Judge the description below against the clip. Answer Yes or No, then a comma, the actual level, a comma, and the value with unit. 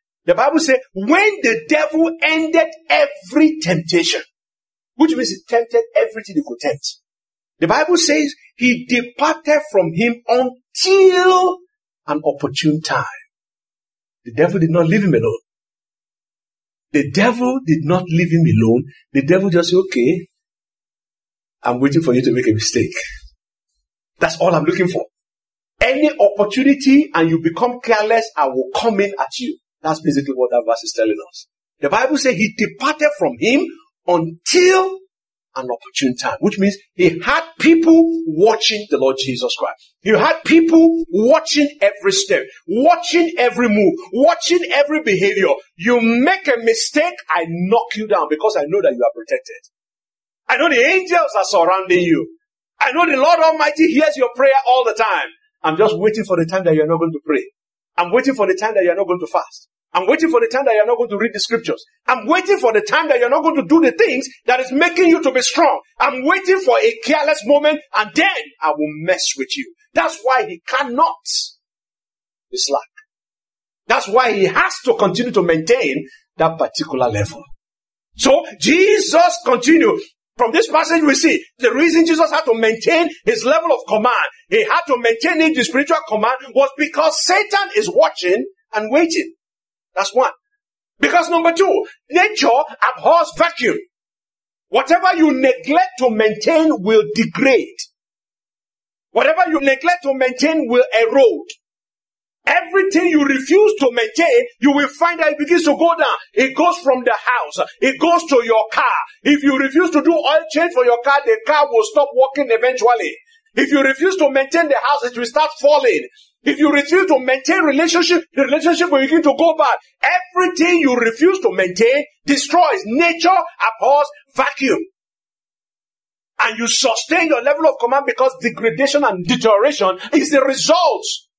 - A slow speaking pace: No, average, 170 wpm